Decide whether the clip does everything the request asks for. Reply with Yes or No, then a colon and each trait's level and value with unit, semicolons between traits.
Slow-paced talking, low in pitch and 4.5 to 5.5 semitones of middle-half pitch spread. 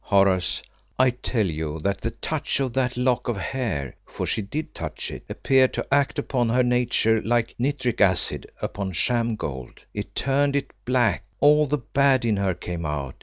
No: average, 180 wpm; low, 120 Hz; average, 5.2 semitones